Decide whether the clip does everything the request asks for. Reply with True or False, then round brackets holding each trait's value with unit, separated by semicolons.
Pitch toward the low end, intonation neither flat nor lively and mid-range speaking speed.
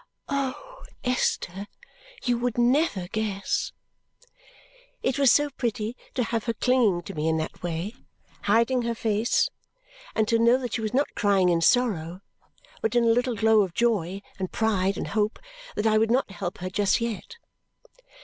False (220 Hz; 3.8 semitones; 170 wpm)